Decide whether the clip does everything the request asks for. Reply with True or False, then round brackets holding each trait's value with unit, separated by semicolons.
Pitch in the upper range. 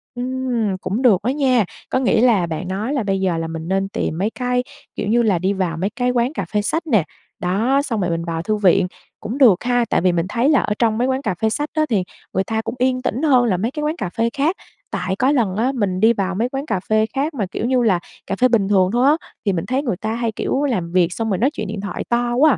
True (220 Hz)